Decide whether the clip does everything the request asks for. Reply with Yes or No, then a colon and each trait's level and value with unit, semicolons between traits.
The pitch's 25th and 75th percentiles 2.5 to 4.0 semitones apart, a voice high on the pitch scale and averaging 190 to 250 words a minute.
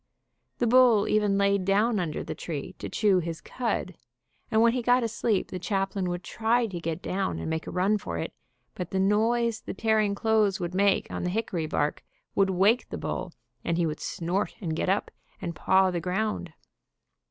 Yes: average, 3.7 semitones; high, 195 Hz; average, 200 wpm